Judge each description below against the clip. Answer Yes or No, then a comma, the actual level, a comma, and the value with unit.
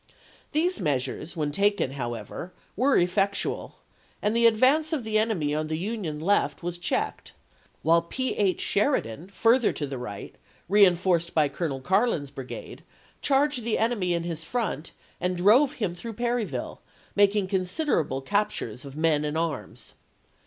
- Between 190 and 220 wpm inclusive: No, average, 150 wpm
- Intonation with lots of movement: Yes, wide, 6.4 semitones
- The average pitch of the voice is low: No, medium, 185 Hz